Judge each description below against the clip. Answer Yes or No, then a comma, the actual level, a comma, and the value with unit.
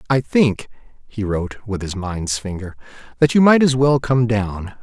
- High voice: No, low, 115 Hz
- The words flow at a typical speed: Yes, average, 185 wpm